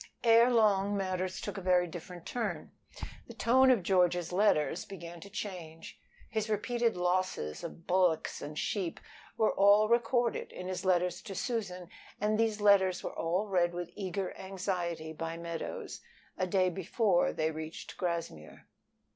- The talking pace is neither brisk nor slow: Yes, average, 150 wpm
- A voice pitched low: No, medium, 185 Hz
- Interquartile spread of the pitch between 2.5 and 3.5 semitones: Yes, average, 3.2 semitones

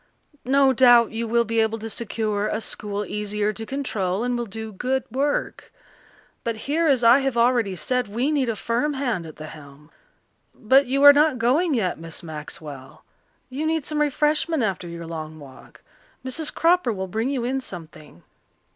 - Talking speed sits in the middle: Yes, average, 180 wpm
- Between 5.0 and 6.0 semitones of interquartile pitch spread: Yes, wide, 5.4 semitones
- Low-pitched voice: No, high, 230 Hz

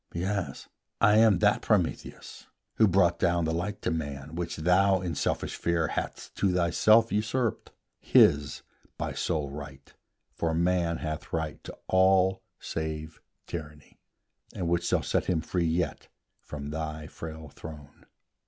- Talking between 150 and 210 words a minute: No, average, 140 wpm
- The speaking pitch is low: Yes, very low, 85 Hz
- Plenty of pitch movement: No, average, 3.0 semitones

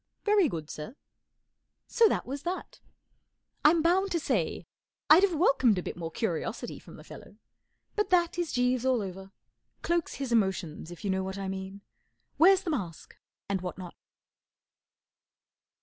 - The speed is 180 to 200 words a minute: No, average, 165 wpm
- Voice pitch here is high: Yes, high, 245 Hz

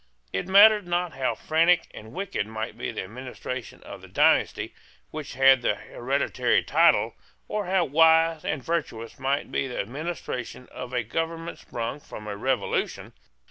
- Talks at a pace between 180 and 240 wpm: No, average, 155 wpm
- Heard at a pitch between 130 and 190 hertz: Yes, medium, 140 Hz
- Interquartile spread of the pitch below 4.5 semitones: No, wide, 5.5 semitones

